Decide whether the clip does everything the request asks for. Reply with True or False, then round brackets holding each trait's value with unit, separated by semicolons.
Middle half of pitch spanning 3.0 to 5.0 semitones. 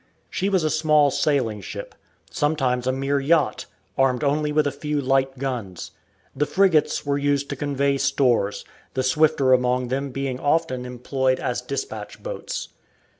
False (2.5 semitones)